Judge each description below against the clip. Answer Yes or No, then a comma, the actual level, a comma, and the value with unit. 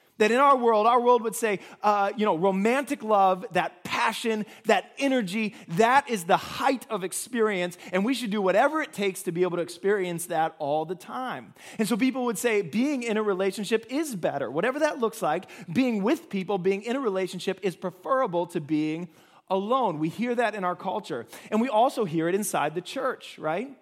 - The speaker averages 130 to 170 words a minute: No, fast, 205 wpm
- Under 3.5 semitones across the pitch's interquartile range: No, average, 4.5 semitones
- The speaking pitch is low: No, high, 210 Hz